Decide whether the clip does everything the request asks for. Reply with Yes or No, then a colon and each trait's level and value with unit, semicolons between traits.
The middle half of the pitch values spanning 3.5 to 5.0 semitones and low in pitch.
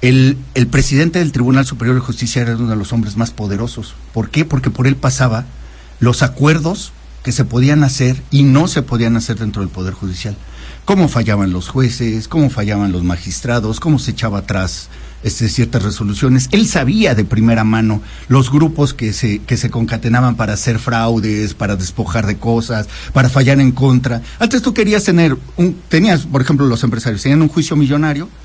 Yes: average, 3.9 semitones; low, 120 Hz